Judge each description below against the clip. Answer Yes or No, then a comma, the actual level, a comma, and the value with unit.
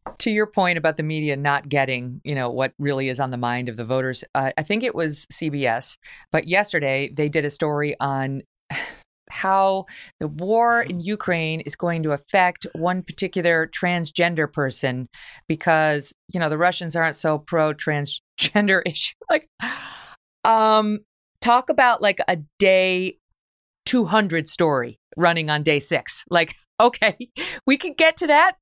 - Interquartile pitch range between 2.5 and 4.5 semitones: No, average, 5.2 semitones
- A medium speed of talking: Yes, average, 155 wpm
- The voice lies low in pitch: No, medium, 165 Hz